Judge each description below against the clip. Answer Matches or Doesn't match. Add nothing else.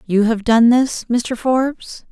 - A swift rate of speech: Doesn't match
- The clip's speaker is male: Doesn't match